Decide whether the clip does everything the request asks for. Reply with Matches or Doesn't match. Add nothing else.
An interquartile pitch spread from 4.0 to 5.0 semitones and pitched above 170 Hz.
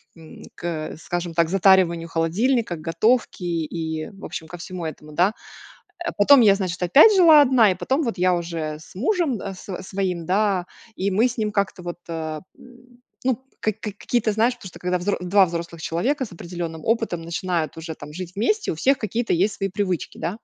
Matches